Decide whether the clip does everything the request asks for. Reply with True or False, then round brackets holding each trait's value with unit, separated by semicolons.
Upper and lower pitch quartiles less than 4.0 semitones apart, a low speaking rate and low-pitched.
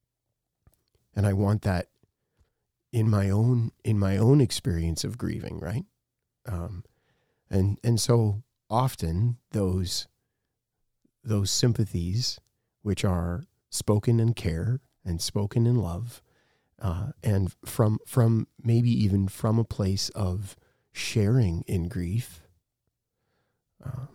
True (3.6 semitones; 110 wpm; 110 Hz)